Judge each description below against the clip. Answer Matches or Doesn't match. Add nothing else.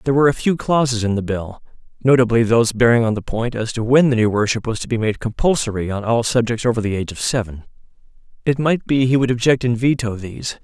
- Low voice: Matches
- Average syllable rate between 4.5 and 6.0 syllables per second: Doesn't match